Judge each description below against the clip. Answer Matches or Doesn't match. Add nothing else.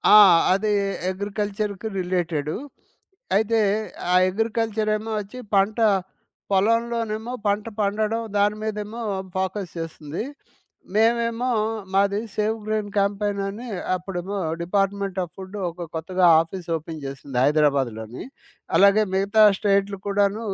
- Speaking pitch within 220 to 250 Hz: Doesn't match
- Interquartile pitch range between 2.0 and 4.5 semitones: Matches